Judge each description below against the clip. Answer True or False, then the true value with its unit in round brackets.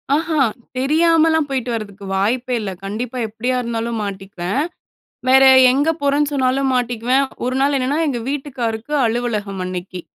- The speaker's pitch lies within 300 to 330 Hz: False (250 Hz)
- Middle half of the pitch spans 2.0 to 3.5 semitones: False (4.2 semitones)